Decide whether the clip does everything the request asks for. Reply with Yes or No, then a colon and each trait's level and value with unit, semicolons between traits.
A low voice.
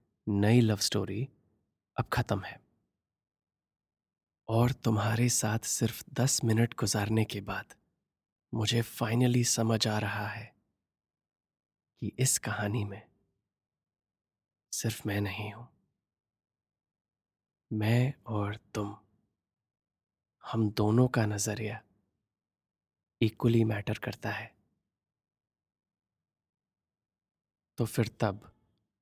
Yes: low, 110 Hz